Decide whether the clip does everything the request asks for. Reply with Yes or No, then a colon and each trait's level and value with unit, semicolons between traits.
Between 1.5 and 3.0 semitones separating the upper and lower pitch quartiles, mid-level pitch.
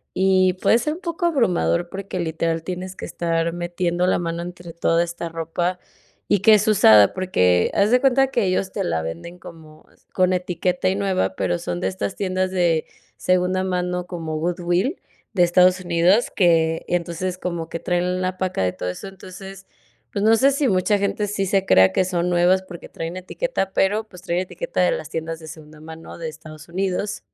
Yes: narrow, 2.4 semitones; medium, 180 Hz